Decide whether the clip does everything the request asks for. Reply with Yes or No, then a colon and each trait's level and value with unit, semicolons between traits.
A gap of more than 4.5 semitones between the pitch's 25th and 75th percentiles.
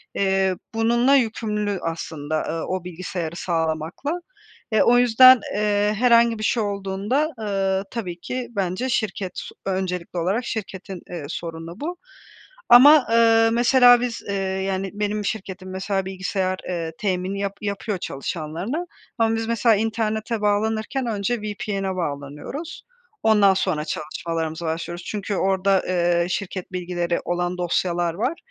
No: average, 4.0 semitones